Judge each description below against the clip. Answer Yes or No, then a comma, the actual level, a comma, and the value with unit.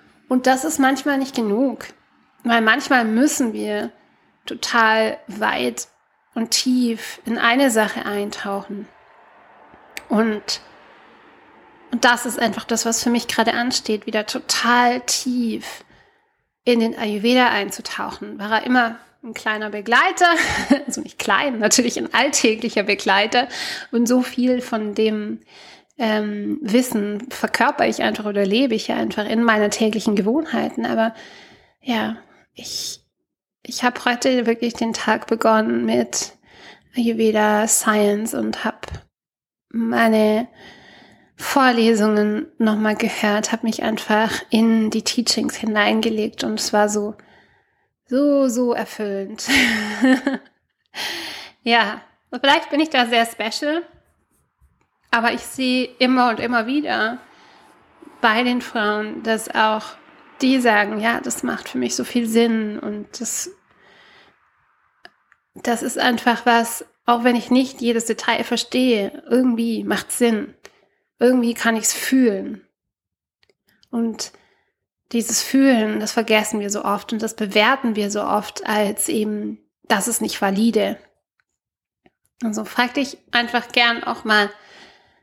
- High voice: Yes, high, 230 Hz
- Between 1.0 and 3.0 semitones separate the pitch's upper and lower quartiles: Yes, narrow, 2.5 semitones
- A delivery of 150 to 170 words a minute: No, slow, 125 wpm